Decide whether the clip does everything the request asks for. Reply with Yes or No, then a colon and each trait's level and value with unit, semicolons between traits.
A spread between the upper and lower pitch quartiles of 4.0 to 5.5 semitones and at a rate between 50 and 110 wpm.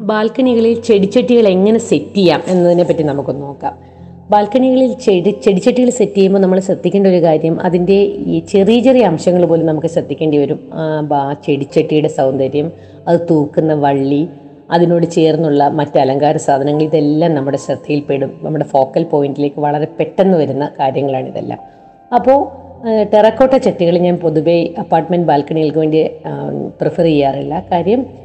No: average, 5.2 semitones; fast, 125 wpm